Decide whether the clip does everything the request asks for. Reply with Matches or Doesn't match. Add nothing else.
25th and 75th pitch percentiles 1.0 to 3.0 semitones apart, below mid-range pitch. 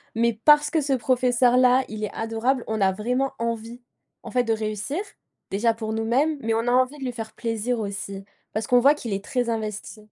Doesn't match